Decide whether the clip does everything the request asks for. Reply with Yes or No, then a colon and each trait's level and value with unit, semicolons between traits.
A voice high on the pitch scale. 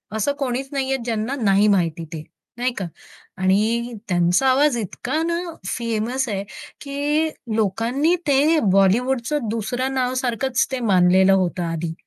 Yes: high, 235 Hz